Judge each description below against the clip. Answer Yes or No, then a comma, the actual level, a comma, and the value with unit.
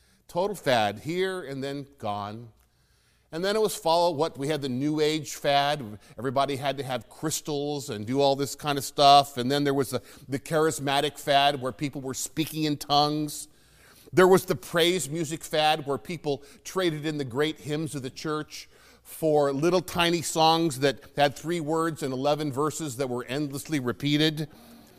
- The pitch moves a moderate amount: No, narrow, 2.3 semitones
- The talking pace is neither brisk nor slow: Yes, average, 180 wpm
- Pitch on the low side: No, medium, 145 Hz